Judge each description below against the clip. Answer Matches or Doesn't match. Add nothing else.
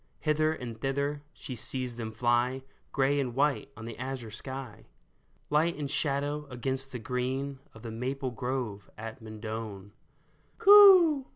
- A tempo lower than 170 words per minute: Matches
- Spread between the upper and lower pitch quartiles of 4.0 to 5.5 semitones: Doesn't match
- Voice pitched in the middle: Doesn't match